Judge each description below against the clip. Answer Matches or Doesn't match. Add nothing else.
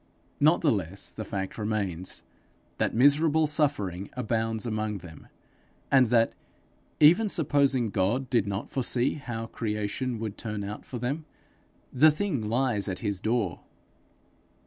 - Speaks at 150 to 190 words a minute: Doesn't match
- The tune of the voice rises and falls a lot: Doesn't match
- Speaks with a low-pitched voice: Matches